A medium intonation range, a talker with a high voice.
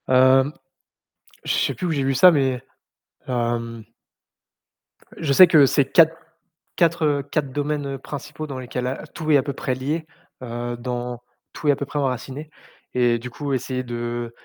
No: average, 3.0 semitones; low, 135 Hz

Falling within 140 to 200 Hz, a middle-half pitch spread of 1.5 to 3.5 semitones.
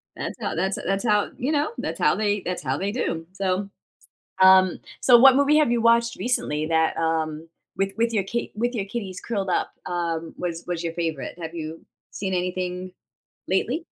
No: high, 190 Hz; wide, 5.6 semitones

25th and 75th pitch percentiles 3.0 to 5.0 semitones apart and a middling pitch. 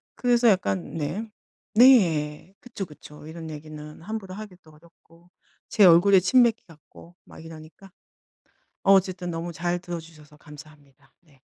Yes: average, 4.0 semitones; medium, 170 Hz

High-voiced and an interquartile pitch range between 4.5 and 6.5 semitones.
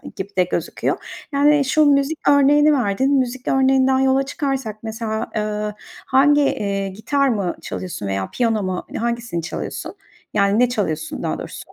Yes: high, 240 Hz; average, 5.2 semitones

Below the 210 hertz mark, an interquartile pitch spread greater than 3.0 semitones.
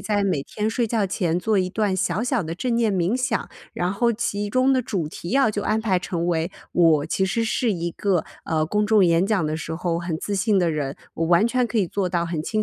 Yes: high, 190 Hz; average, 4.4 semitones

